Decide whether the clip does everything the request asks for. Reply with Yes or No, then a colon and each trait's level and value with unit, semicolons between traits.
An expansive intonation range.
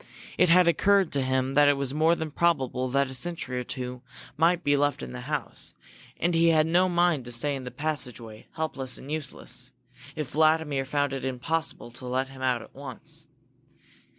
No: average, 3.9 semitones